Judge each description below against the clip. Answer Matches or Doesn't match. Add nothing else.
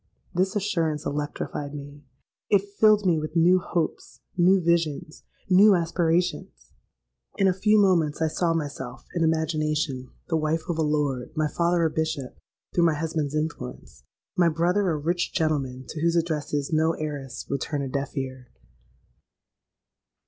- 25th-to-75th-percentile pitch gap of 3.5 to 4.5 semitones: Doesn't match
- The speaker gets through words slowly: Doesn't match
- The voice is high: Doesn't match